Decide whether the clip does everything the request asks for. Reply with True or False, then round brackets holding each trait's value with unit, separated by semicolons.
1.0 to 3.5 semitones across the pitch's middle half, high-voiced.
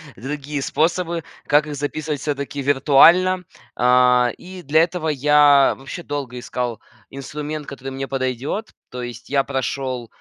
False (2.6 semitones; 140 Hz)